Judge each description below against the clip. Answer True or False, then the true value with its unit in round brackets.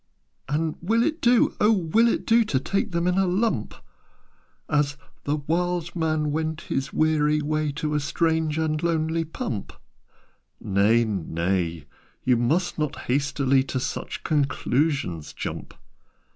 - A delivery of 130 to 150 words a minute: True (140 wpm)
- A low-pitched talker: False (155 Hz)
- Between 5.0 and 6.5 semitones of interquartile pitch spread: False (3.9 semitones)